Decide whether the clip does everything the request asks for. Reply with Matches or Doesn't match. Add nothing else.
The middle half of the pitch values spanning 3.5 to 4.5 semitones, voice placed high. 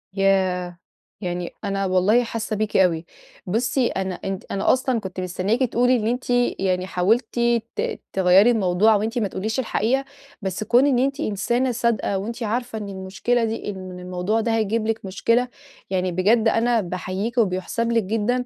Matches